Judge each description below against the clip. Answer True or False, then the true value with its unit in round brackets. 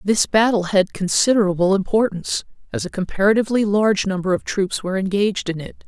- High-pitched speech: True (200 Hz)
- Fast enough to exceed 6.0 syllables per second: True (6.2 syllables/s)